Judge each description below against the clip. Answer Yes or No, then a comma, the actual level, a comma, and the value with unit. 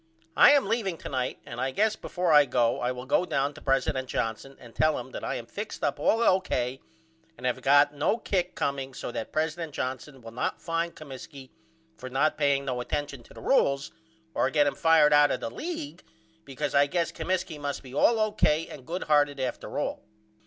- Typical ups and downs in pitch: Yes, average, 4.1 semitones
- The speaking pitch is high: No, medium, 145 Hz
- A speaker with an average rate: No, fast, 210 wpm